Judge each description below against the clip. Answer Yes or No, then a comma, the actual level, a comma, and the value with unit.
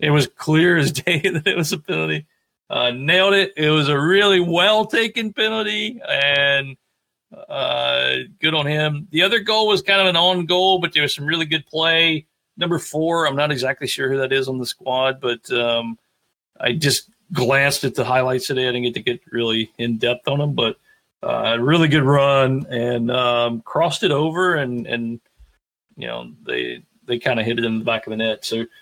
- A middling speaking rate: No, fast, 210 wpm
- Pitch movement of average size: No, wide, 5.9 semitones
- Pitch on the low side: No, medium, 145 Hz